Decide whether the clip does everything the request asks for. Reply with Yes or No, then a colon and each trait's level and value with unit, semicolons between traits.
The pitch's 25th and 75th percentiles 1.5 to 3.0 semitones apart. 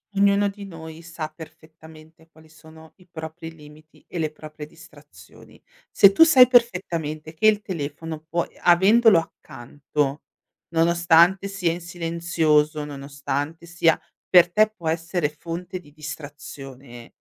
Yes: narrow, 2.4 semitones